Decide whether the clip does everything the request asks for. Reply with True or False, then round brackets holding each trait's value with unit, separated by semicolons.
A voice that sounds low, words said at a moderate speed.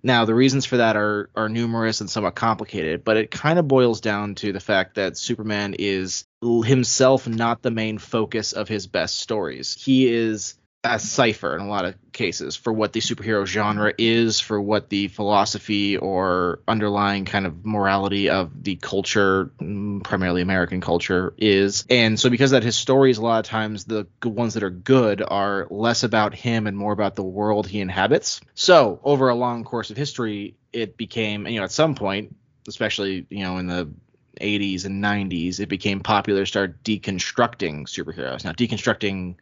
True (105 Hz; 185 wpm)